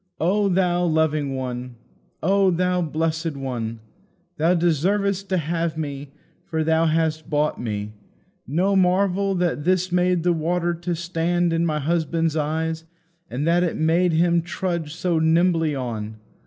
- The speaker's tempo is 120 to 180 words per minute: Yes, average, 145 wpm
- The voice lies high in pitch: No, medium, 165 Hz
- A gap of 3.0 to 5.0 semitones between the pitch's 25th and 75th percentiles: No, narrow, 2.5 semitones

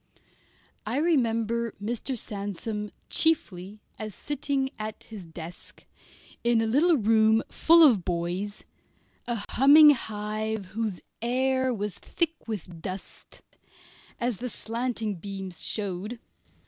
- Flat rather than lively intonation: No, average, 3.7 semitones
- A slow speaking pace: Yes, slow, 110 wpm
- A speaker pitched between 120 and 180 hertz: No, high, 220 Hz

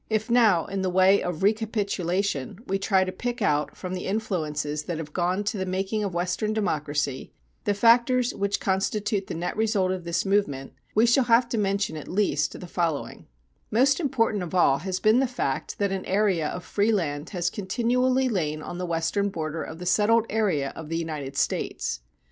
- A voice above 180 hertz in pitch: Yes, high, 190 Hz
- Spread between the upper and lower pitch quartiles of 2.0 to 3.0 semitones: No, average, 4.5 semitones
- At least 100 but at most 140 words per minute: No, average, 195 wpm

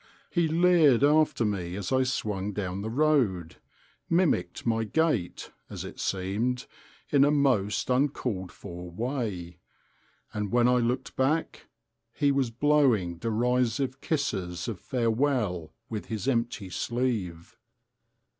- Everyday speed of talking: No, slow, 120 wpm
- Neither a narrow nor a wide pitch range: No, wide, 6.1 semitones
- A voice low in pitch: Yes, low, 120 Hz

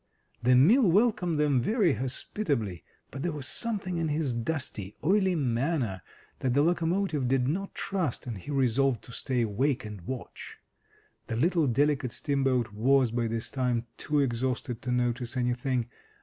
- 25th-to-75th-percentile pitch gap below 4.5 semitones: No, average, 4.8 semitones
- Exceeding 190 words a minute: No, average, 155 wpm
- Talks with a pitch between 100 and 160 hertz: Yes, low, 135 Hz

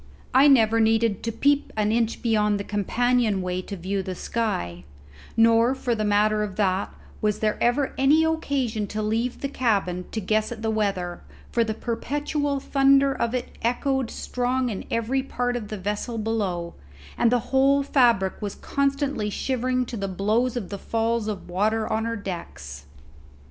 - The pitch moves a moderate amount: Yes, average, 3.5 semitones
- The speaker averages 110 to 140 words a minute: No, average, 175 wpm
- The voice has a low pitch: No, high, 225 Hz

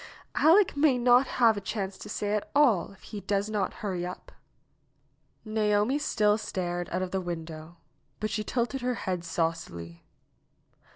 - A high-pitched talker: Yes, high, 205 Hz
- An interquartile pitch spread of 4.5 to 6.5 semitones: Yes, average, 5.0 semitones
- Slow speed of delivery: No, average, 160 wpm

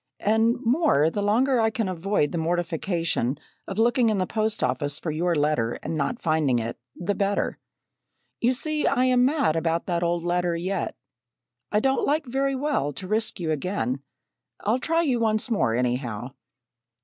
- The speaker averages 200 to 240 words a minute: No, average, 175 wpm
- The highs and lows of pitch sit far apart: Yes, wide, 6.8 semitones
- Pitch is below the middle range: No, high, 190 Hz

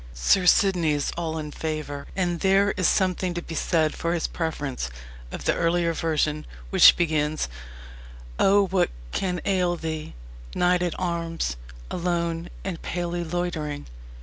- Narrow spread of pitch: Yes, narrow, 2.2 semitones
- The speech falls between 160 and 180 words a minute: No, average, 145 wpm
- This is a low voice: No, medium, 170 Hz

